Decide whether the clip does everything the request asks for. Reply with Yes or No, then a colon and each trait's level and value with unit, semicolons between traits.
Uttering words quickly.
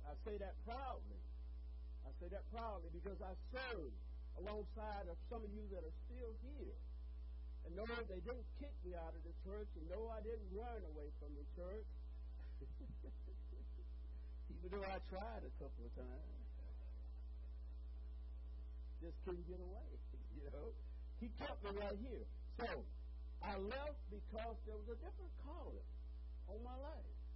No: average, 155 wpm